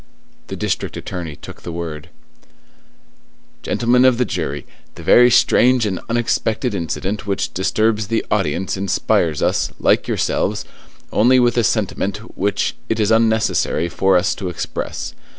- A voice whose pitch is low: Yes, low, 105 Hz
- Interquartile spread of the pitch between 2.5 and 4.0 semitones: No, average, 4.6 semitones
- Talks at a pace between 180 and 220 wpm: No, average, 140 wpm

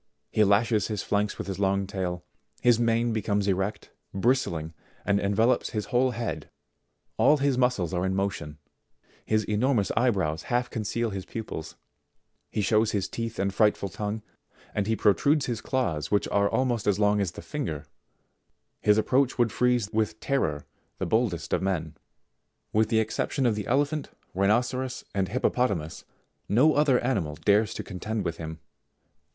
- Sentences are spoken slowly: No, average, 165 wpm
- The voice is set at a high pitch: No, low, 105 Hz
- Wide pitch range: No, average, 3.8 semitones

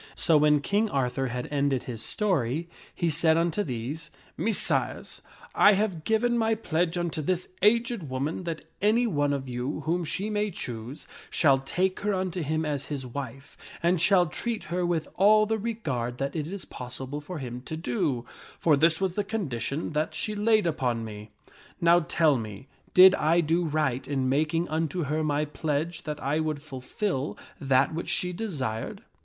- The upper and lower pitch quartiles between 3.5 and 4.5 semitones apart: No, average, 5.1 semitones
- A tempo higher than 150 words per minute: Yes, average, 180 wpm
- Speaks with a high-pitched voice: No, medium, 155 Hz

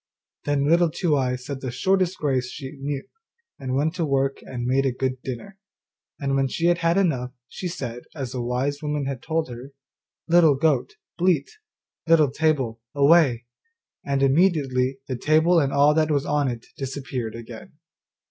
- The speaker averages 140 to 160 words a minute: No, average, 170 wpm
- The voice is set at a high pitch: No, medium, 140 Hz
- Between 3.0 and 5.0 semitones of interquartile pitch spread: Yes, average, 3.5 semitones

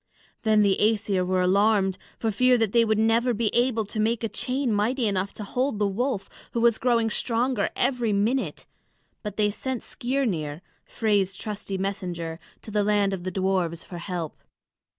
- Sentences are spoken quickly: No, average, 175 wpm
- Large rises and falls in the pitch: No, average, 3.3 semitones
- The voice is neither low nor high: No, high, 210 Hz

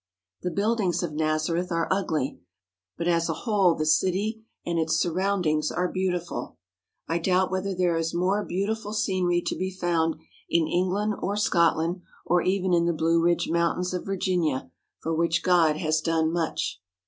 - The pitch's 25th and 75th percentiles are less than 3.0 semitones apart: Yes, narrow, 2.4 semitones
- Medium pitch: Yes, medium, 175 Hz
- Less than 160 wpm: No, average, 170 wpm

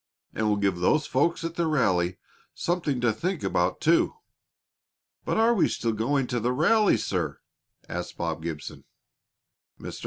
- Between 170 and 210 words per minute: No, average, 160 wpm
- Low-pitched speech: Yes, low, 125 Hz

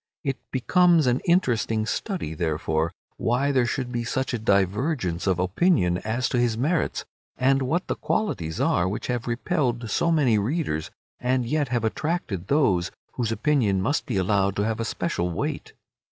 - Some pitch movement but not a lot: No, wide, 6.0 semitones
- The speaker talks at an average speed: Yes, average, 165 wpm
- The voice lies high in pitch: No, low, 120 Hz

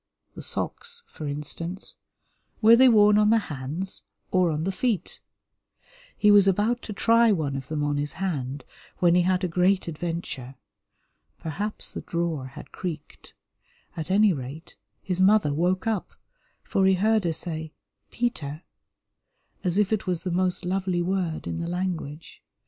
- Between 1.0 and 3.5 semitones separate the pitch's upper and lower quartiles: No, average, 4.2 semitones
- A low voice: No, medium, 180 Hz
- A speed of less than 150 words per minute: No, average, 160 wpm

